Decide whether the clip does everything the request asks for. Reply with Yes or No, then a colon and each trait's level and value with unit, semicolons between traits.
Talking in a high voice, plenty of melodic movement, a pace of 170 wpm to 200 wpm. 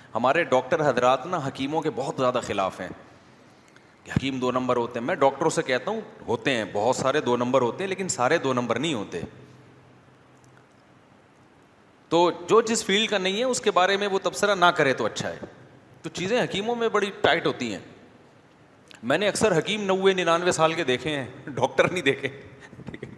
No: medium, 165 Hz; wide, 7.2 semitones; fast, 190 wpm